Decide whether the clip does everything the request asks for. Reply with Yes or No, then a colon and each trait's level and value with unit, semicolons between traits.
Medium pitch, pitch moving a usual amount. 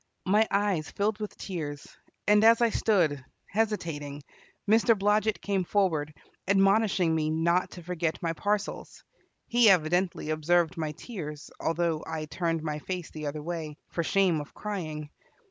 Yes: medium, 175 Hz; average, 4.6 semitones